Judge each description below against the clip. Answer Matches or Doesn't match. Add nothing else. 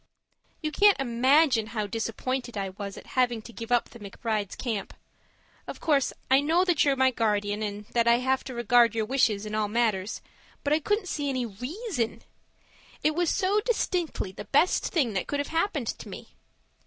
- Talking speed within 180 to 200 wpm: Matches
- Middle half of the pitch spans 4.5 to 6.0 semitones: Matches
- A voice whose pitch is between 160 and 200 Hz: Doesn't match